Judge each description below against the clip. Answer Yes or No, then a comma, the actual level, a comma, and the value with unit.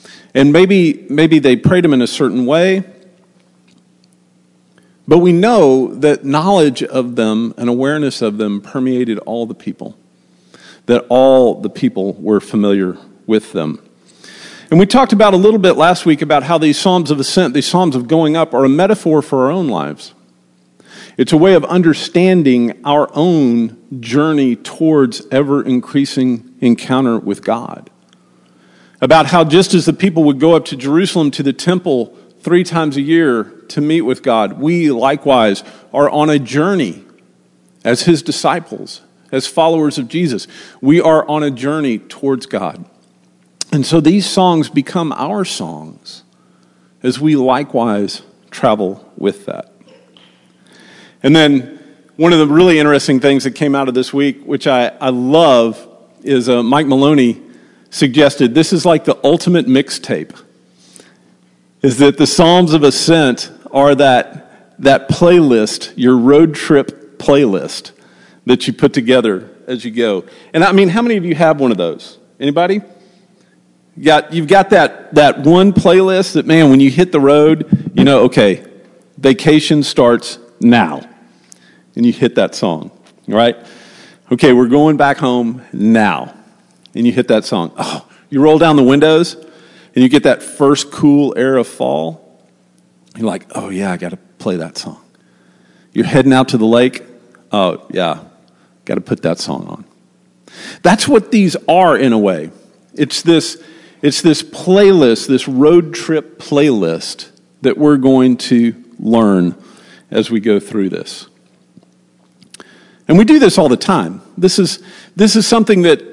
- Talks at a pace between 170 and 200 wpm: No, average, 160 wpm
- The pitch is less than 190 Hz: Yes, medium, 140 Hz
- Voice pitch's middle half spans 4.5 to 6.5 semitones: Yes, wide, 5.4 semitones